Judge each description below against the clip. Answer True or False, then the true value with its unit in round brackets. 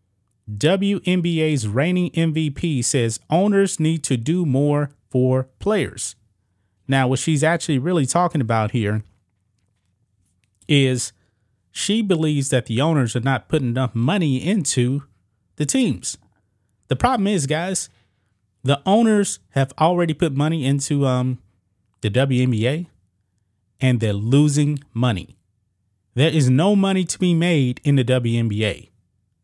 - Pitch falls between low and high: False (130 Hz)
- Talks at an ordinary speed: False (125 wpm)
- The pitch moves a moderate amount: False (6.8 semitones)